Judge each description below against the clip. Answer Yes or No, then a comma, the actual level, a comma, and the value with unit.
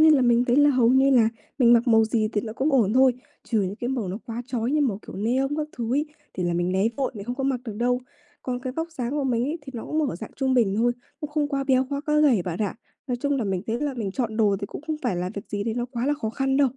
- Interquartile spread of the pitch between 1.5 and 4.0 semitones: Yes, average, 3.7 semitones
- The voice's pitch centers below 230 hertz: No, high, 245 Hz